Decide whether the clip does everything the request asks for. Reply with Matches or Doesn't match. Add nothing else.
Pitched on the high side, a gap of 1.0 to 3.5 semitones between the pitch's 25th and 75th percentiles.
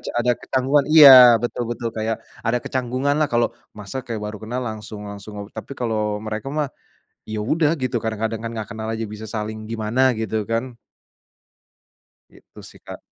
Doesn't match